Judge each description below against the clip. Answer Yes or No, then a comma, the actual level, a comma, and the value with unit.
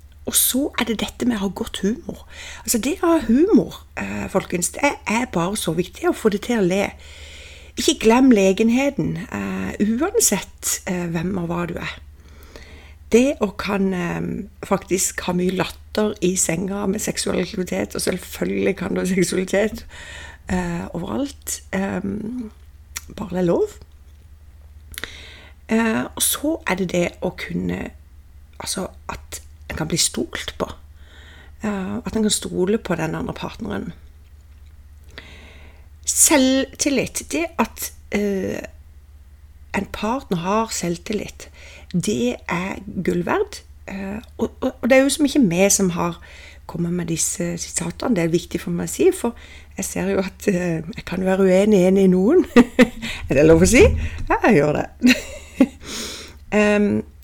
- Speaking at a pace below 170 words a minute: Yes, average, 150 wpm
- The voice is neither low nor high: Yes, medium, 180 Hz